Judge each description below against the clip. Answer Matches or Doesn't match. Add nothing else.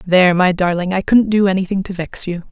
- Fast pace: Matches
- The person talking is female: Matches